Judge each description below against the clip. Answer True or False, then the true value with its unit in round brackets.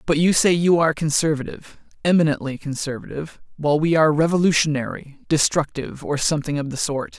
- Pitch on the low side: False (155 Hz)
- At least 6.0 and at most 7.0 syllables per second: True (6.4 syllables/s)